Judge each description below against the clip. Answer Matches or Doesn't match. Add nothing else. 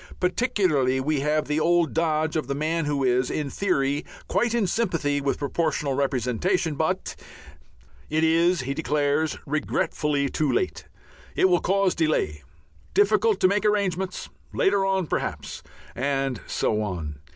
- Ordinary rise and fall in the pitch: Matches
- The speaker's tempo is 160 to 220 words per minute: Doesn't match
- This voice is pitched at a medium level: Matches